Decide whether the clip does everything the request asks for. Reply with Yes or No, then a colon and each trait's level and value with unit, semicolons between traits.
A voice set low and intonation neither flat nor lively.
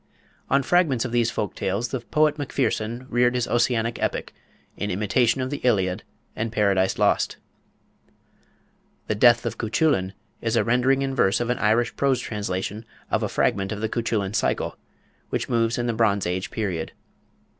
Yes: low, 115 Hz; average, 3.1 semitones